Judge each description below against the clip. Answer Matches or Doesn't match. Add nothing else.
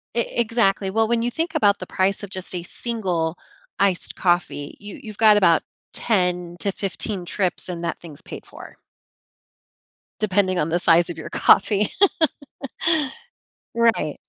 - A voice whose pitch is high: Matches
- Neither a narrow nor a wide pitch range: Matches